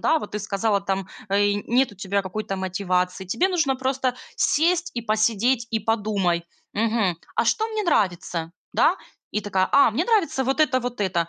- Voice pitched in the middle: No, high, 215 Hz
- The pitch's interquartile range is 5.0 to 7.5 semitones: Yes, wide, 5.5 semitones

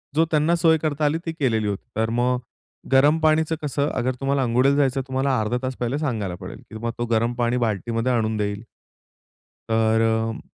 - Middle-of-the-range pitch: No, low, 125 Hz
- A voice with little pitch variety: No, average, 4.3 semitones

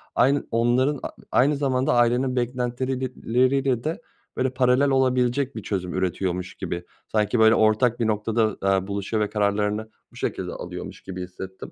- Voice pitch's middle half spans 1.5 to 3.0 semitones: No, average, 3.9 semitones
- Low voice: Yes, low, 120 Hz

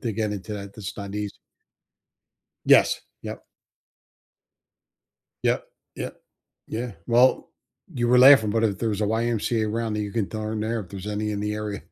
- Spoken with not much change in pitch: Yes, narrow, 1.8 semitones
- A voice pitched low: Yes, low, 110 Hz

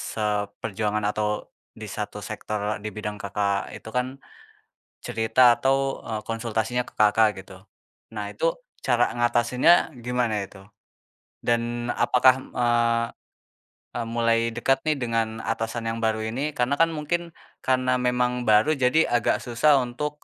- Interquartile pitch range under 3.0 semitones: Yes, narrow, 2.5 semitones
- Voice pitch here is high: No, low, 120 Hz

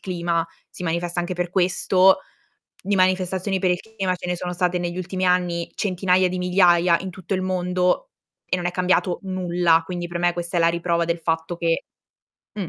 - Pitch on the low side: No, medium, 180 Hz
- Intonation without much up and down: Yes, narrow, 1.2 semitones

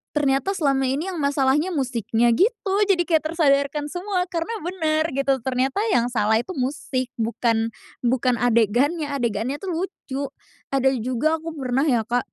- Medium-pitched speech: No, very high, 275 Hz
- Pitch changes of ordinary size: Yes, average, 4.7 semitones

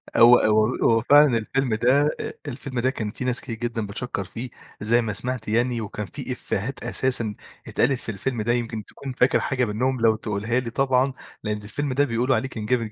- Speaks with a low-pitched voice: Yes, low, 120 Hz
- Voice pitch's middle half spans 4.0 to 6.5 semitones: No, average, 3.0 semitones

